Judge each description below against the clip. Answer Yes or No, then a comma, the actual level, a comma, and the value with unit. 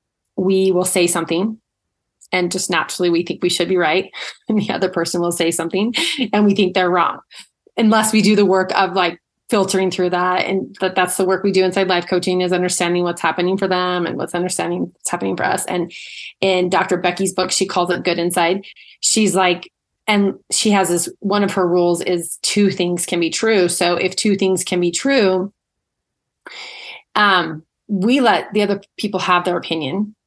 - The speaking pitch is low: No, medium, 185 Hz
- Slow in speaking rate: No, average, 200 wpm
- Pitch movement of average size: No, narrow, 1.9 semitones